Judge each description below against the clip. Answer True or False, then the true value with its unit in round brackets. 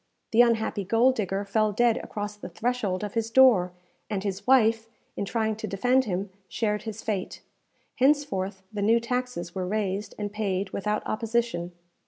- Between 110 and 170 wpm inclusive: True (165 wpm)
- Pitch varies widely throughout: False (2.9 semitones)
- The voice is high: True (215 Hz)